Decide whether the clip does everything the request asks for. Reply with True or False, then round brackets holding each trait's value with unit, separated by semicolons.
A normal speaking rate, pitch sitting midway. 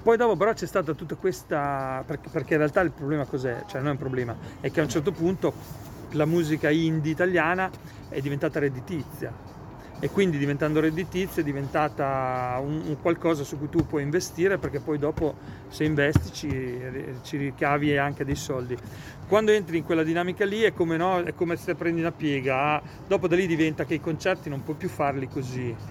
False (195 wpm; 155 Hz)